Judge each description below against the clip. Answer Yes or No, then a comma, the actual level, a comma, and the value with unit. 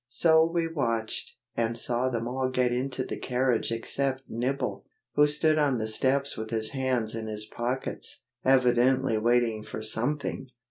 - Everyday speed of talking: Yes, average, 155 wpm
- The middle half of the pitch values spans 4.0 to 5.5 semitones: No, average, 2.8 semitones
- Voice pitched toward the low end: Yes, low, 125 Hz